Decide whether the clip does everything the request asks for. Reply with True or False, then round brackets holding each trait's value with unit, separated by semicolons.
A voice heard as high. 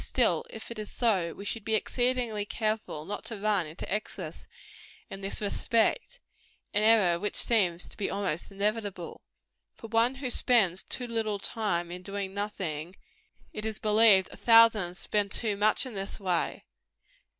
True (210 Hz)